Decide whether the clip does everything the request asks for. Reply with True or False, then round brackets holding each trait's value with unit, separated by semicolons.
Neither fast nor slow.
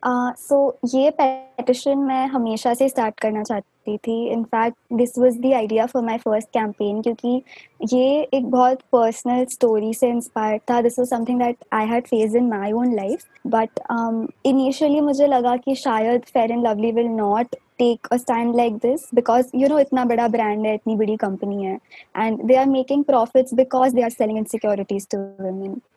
True (160 wpm)